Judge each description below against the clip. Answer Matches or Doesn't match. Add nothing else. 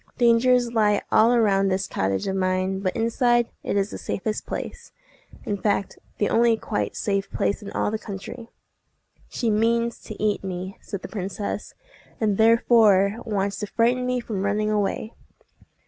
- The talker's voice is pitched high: Matches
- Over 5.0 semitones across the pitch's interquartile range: Doesn't match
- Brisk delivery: Doesn't match